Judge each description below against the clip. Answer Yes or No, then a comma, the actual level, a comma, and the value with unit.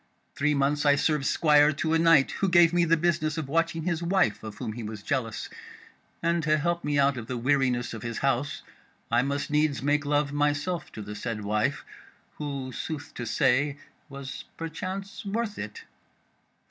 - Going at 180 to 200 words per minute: Yes, average, 185 wpm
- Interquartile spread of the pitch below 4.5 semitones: Yes, average, 3.8 semitones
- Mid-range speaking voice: Yes, medium, 145 Hz